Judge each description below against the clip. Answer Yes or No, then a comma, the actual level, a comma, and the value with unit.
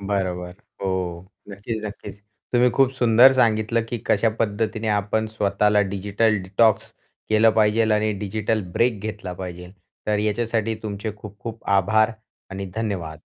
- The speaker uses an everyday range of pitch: No, narrow, 2.2 semitones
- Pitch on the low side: Yes, low, 105 Hz